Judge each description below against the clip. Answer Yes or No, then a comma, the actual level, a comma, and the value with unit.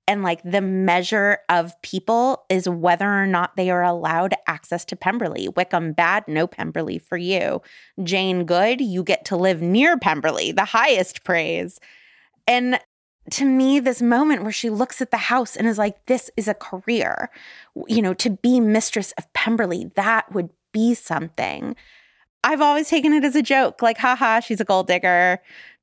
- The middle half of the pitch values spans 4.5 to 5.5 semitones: Yes, average, 4.9 semitones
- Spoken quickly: No, average, 175 wpm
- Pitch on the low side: No, high, 205 Hz